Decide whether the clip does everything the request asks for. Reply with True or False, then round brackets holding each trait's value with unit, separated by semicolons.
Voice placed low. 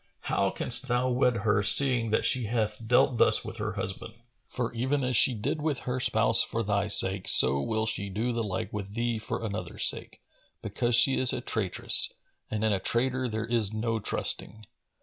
True (115 Hz)